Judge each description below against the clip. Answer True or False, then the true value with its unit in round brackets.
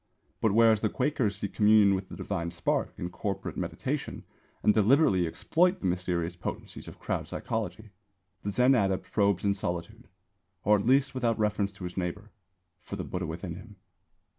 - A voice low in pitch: True (100 Hz)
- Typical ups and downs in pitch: True (3.5 semitones)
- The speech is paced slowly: False (170 wpm)